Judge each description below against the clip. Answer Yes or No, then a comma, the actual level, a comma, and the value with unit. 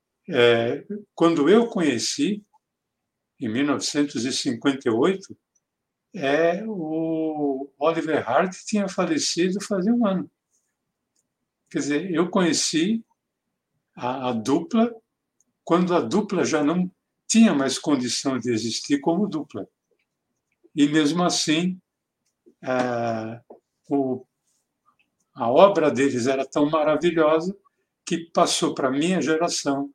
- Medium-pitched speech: Yes, medium, 160 Hz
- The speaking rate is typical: No, slow, 100 wpm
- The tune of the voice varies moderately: Yes, average, 5.0 semitones